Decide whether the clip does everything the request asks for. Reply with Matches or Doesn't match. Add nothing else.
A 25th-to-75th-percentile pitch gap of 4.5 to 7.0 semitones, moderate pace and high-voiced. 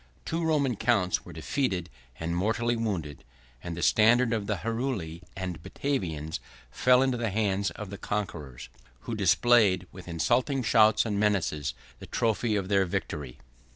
Doesn't match